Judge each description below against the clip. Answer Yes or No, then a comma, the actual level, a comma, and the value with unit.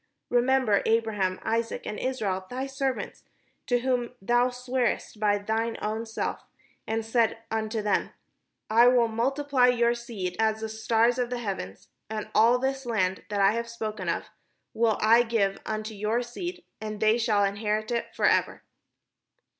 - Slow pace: No, average, 155 wpm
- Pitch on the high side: Yes, high, 225 Hz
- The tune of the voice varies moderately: No, narrow, 2.3 semitones